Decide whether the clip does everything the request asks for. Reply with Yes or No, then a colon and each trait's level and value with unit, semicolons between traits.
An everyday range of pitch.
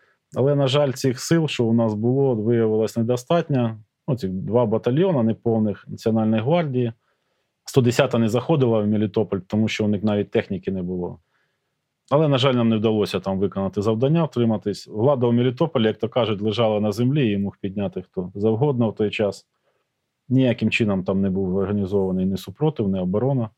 Yes: average, 3.9 semitones